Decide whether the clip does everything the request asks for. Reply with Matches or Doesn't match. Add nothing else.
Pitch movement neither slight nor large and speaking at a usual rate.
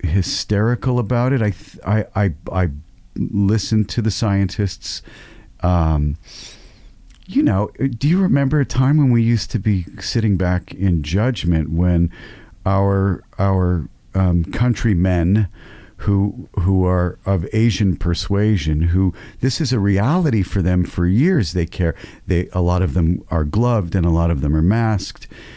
Matches